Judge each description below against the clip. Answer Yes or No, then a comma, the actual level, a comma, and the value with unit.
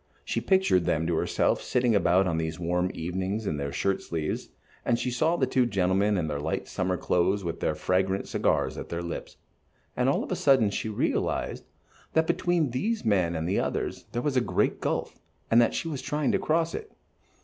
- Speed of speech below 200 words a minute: No, fast, 205 wpm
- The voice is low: Yes, low, 100 Hz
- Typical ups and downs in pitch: No, wide, 6.7 semitones